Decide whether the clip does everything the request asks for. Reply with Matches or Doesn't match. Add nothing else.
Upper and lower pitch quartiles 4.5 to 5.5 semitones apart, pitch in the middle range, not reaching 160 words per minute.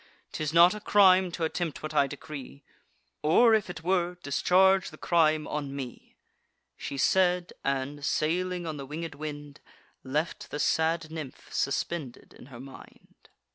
Doesn't match